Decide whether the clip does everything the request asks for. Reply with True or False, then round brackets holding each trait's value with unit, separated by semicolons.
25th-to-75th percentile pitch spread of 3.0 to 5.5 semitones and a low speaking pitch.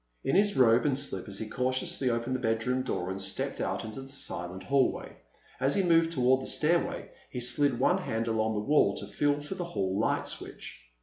True (4.7 semitones; 125 Hz)